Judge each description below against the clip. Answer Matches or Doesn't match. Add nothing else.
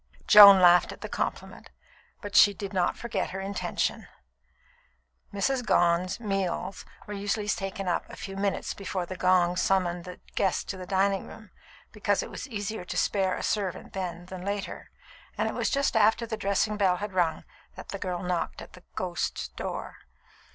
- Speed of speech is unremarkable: Matches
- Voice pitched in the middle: Doesn't match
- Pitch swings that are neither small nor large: Doesn't match